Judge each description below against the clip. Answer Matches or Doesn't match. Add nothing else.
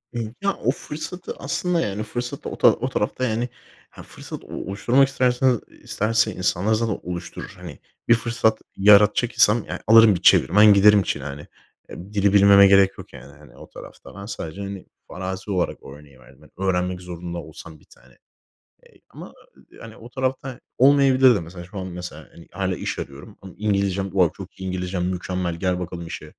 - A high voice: Doesn't match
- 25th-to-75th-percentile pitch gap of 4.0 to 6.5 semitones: Matches